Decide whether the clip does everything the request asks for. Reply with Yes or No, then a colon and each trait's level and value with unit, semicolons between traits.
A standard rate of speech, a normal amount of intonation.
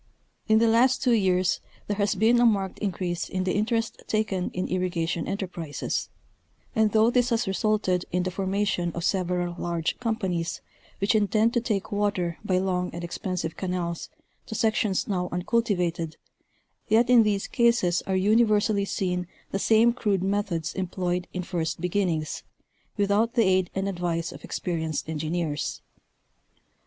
Yes: average, 155 wpm; average, 3.4 semitones